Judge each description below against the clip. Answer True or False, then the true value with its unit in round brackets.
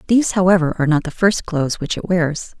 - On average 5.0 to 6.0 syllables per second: False (6.3 syllables/s)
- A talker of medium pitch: True (175 Hz)